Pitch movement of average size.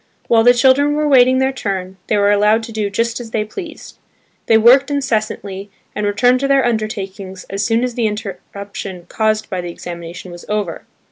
Yes: average, 3.7 semitones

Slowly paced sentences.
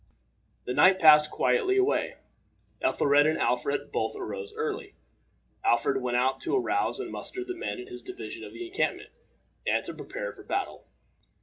No: average, 165 wpm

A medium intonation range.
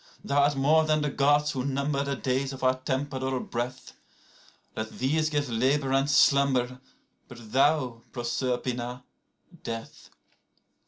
No: narrow, 2.3 semitones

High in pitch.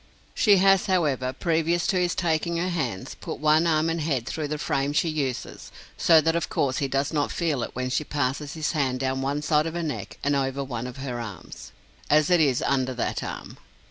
No: medium, 150 Hz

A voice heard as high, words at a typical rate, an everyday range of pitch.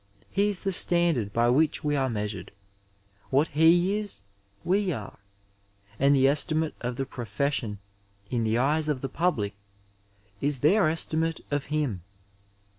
No: medium, 145 Hz; average, 155 wpm; average, 4.9 semitones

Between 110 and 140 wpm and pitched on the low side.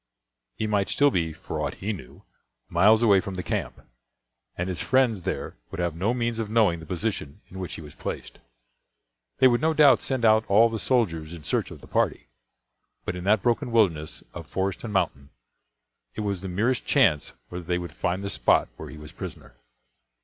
No: average, 200 wpm; low, 100 Hz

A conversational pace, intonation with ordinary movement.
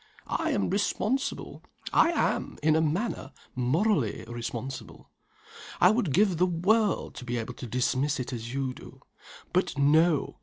No: average, 150 wpm; wide, 7.0 semitones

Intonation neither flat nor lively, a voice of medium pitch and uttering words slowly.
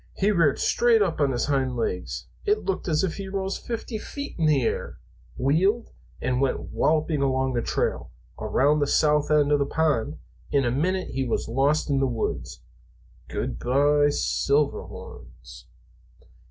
No: average, 4.1 semitones; medium, 145 Hz; average, 165 wpm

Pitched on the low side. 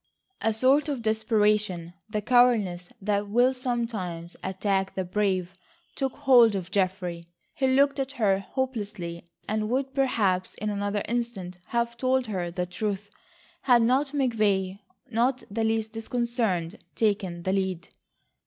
No: high, 215 Hz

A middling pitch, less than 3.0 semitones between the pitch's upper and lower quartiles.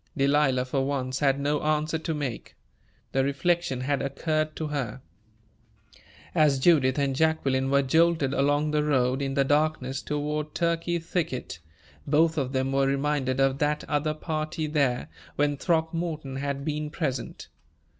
Yes: medium, 145 Hz; narrow, 2.4 semitones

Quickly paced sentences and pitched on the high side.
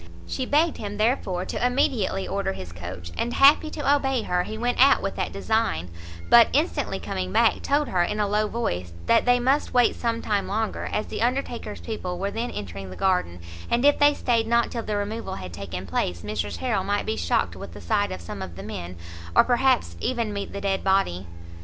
Yes: fast, 215 wpm; high, 210 Hz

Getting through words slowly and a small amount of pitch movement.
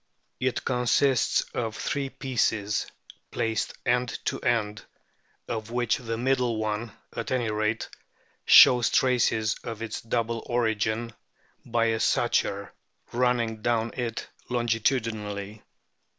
Yes: slow, 110 wpm; narrow, 1.9 semitones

